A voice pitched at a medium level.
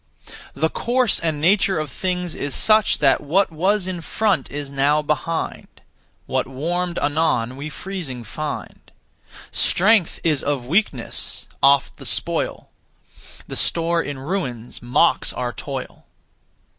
Yes: medium, 155 Hz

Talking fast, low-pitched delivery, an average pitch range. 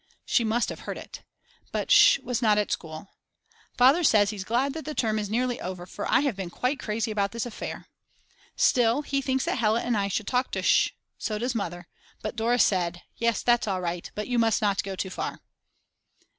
No: fast, 210 wpm; high, 220 Hz; average, 3.7 semitones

